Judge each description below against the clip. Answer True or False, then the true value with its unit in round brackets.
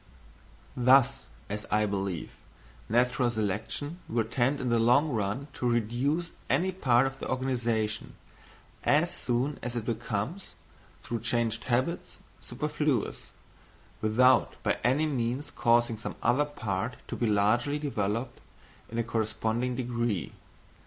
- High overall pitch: False (120 Hz)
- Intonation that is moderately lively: True (3.3 semitones)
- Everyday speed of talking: False (125 wpm)